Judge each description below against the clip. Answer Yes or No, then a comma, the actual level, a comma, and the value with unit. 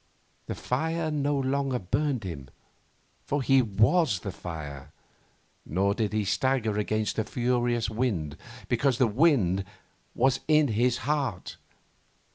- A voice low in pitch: Yes, low, 120 Hz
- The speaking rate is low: Yes, slow, 125 wpm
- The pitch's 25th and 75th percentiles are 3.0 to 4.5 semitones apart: No, average, 5.3 semitones